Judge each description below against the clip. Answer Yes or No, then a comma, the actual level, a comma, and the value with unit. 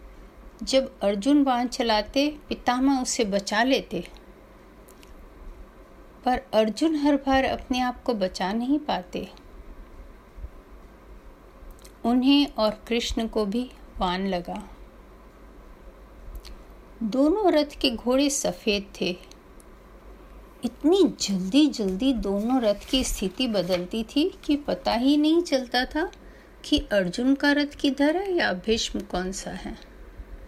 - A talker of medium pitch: No, very high, 250 Hz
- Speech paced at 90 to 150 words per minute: Yes, slow, 110 wpm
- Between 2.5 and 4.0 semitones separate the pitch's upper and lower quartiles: No, wide, 5.5 semitones